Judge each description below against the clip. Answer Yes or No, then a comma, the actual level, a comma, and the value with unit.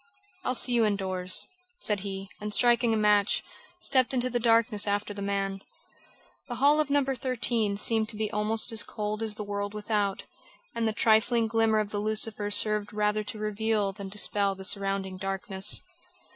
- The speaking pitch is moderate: No, high, 210 Hz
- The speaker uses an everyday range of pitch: No, narrow, 1.9 semitones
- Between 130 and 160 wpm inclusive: No, average, 175 wpm